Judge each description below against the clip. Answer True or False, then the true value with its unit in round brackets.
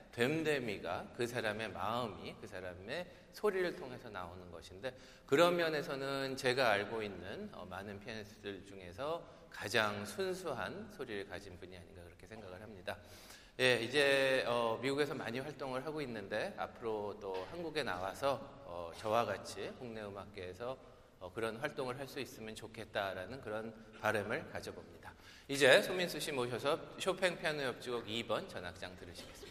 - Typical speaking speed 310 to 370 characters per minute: True (345 characters per minute)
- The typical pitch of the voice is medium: False (115 Hz)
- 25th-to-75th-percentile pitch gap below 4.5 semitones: False (5.4 semitones)